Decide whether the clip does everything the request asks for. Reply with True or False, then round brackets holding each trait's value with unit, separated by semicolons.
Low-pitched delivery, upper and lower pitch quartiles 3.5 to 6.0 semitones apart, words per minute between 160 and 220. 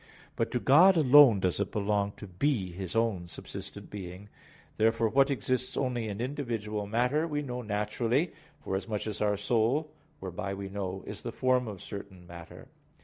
True (110 Hz; 4.4 semitones; 165 wpm)